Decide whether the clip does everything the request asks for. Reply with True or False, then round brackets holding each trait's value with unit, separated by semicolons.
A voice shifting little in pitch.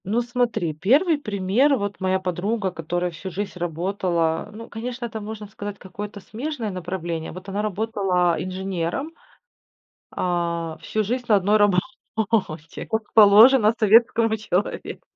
False (3.7 semitones)